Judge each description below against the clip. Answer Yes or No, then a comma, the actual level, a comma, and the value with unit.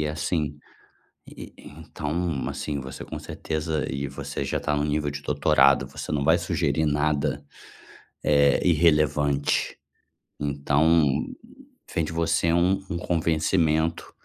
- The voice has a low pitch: Yes, very low, 75 Hz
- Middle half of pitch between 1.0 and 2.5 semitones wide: Yes, narrow, 2.2 semitones